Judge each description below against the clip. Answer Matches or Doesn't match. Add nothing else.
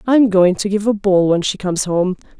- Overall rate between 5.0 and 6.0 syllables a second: Matches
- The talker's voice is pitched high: Matches